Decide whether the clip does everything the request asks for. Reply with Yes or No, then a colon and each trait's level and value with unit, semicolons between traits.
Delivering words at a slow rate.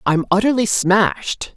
Yes: slow, 115 wpm